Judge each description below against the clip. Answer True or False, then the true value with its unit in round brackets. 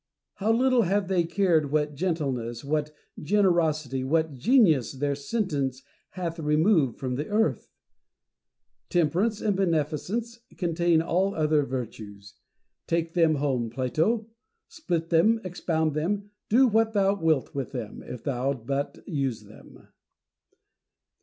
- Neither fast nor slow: False (125 wpm)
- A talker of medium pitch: True (160 Hz)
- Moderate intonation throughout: False (5.8 semitones)